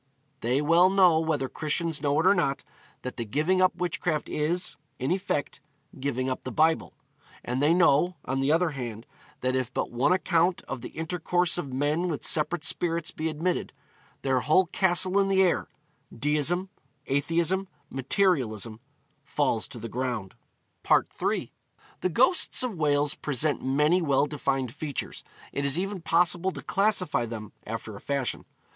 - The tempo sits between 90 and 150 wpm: No, average, 160 wpm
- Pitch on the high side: No, medium, 150 Hz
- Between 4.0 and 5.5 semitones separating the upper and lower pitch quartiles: Yes, average, 4.9 semitones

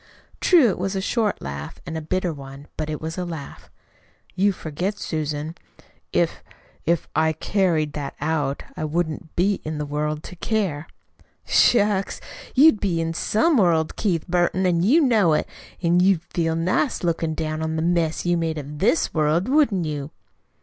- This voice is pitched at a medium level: Yes, medium, 165 Hz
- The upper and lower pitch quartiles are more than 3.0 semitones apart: Yes, average, 3.7 semitones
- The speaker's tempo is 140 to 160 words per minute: No, average, 175 wpm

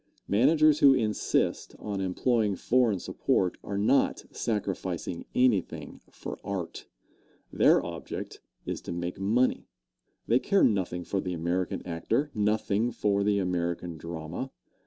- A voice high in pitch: No, low, 100 Hz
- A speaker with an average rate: No, slow, 125 wpm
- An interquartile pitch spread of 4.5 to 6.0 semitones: Yes, average, 4.8 semitones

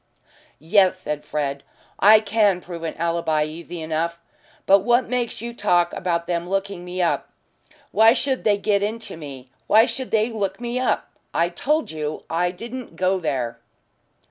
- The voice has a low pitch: No, medium, 185 Hz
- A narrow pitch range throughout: No, average, 4.9 semitones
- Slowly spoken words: No, average, 165 wpm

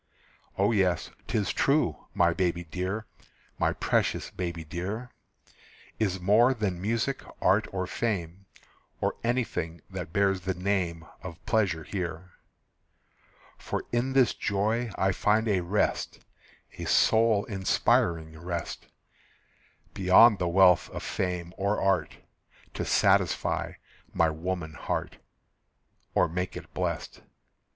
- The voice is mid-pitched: No, very low, 95 Hz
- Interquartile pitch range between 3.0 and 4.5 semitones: Yes, average, 3.6 semitones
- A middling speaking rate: No, slow, 120 wpm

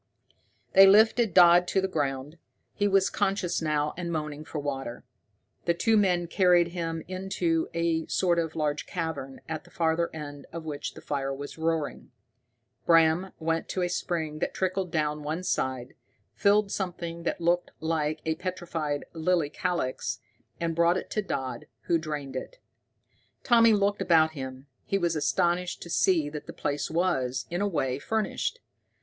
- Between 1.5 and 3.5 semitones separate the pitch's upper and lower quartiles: Yes, average, 3.2 semitones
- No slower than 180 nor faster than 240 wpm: No, average, 165 wpm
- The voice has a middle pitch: Yes, medium, 165 Hz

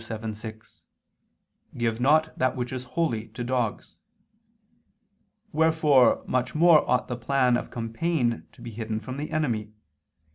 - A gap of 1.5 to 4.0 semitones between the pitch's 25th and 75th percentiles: No, average, 4.4 semitones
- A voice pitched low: Yes, low, 125 Hz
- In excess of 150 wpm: No, slow, 135 wpm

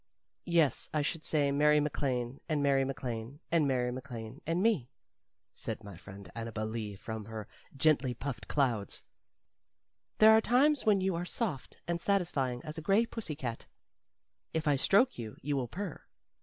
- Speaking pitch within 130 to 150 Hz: Yes, medium, 140 Hz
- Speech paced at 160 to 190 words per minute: Yes, average, 165 wpm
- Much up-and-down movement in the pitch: Yes, wide, 6.0 semitones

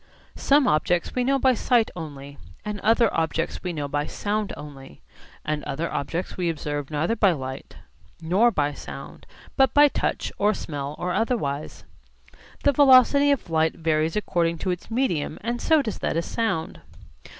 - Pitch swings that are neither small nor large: No, wide, 7.3 semitones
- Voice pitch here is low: No, medium, 175 Hz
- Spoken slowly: No, average, 165 wpm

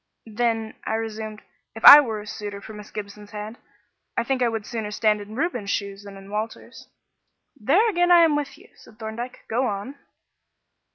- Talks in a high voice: Yes, high, 220 Hz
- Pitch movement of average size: Yes, average, 3.3 semitones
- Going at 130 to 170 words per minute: No, average, 185 wpm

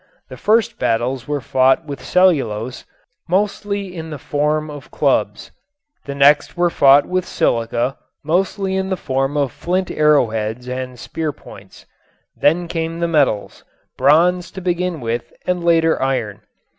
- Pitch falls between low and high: Yes, medium, 150 Hz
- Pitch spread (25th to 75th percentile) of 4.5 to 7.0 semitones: Yes, average, 5.3 semitones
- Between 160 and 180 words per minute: No, average, 145 wpm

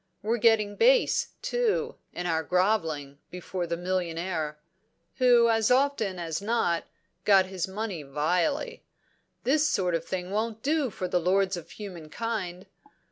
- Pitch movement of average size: Yes, average, 4.8 semitones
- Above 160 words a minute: No, average, 145 wpm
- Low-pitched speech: No, high, 190 Hz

